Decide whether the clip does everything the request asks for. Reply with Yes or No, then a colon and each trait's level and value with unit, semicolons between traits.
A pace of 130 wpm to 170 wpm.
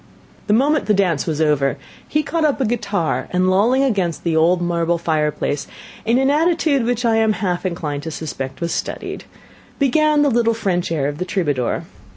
No: average, 190 wpm